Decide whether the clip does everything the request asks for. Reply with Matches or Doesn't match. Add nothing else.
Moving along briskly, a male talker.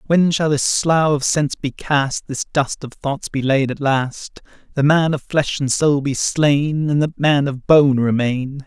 Matches